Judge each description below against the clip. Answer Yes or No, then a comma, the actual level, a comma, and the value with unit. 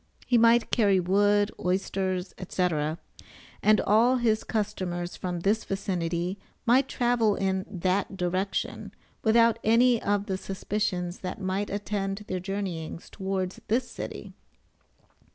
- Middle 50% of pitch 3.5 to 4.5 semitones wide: No, average, 2.7 semitones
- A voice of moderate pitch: No, high, 195 Hz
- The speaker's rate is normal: No, slow, 120 wpm